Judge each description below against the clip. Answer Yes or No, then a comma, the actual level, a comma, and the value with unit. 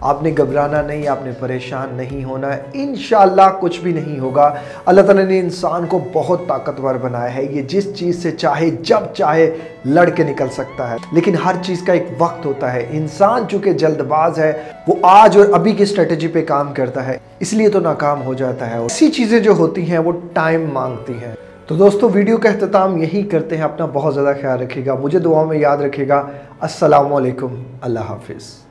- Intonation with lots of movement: No, average, 4.6 semitones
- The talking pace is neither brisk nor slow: No, fast, 205 wpm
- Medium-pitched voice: Yes, medium, 155 Hz